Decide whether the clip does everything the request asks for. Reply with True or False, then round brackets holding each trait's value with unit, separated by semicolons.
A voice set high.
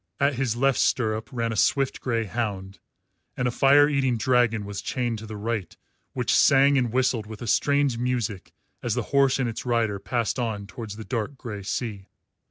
False (120 Hz)